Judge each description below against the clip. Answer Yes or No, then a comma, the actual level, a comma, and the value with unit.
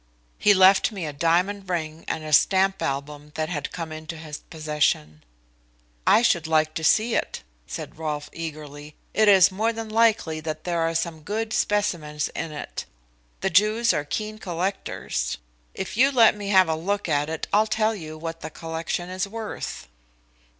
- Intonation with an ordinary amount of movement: Yes, average, 4.7 semitones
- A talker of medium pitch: Yes, medium, 165 Hz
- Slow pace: No, average, 175 wpm